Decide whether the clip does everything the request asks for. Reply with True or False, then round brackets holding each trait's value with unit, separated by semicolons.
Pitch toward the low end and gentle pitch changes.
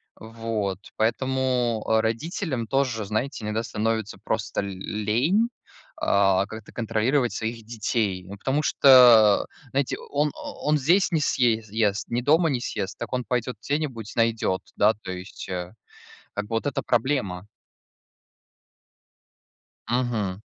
False (115 Hz; 3.8 semitones)